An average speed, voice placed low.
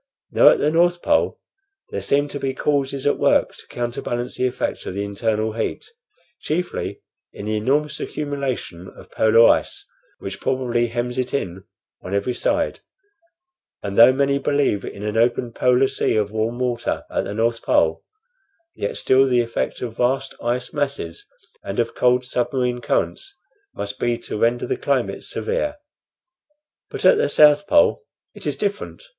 Yes: average, 165 wpm; low, 125 Hz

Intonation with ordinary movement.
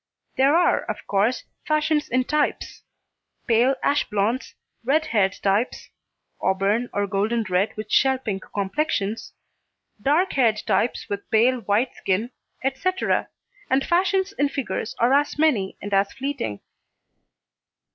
No: wide, 6.0 semitones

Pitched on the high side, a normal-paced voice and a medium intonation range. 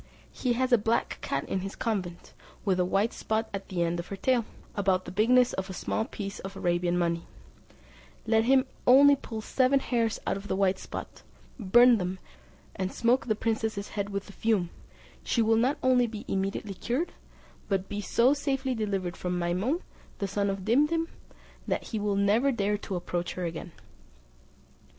Yes: high, 205 Hz; average, 185 wpm; average, 4.2 semitones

